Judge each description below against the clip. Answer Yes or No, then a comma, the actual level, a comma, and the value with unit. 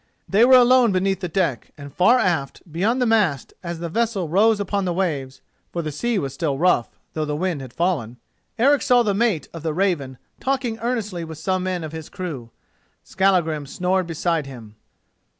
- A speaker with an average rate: Yes, average, 185 wpm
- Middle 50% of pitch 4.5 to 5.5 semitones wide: Yes, average, 5.1 semitones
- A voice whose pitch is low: No, medium, 180 Hz